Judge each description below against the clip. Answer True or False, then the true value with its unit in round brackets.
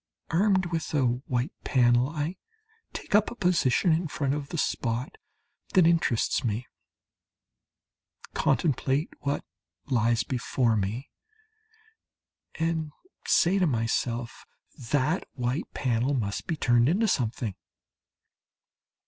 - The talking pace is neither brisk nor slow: False (110 wpm)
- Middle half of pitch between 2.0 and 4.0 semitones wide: False (5.4 semitones)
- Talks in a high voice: False (135 Hz)